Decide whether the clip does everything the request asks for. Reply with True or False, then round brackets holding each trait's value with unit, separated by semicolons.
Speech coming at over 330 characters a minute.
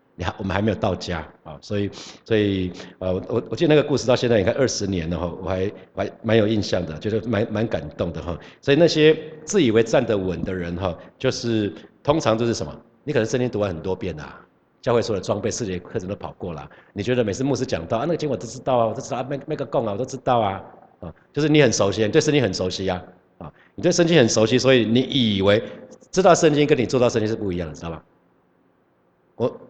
True (355 characters per minute)